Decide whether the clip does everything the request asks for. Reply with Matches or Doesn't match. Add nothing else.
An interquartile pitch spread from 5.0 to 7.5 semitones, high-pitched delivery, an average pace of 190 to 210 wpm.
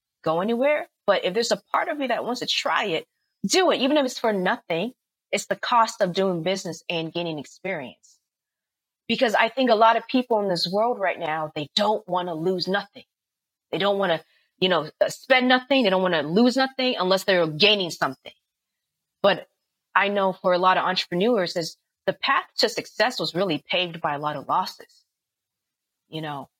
Matches